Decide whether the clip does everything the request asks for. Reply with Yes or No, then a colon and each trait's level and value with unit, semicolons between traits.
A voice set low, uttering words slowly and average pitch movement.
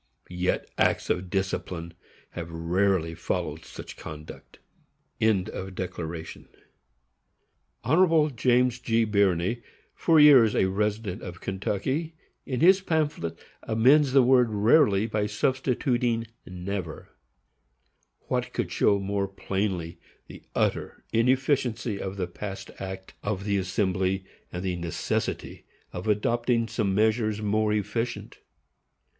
Yes: low, 105 Hz; slow, 110 wpm; average, 3.9 semitones